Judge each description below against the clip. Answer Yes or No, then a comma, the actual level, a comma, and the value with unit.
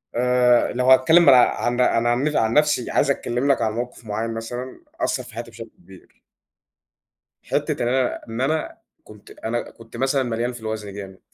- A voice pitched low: Yes, low, 120 Hz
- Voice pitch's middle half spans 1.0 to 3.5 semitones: Yes, narrow, 2.4 semitones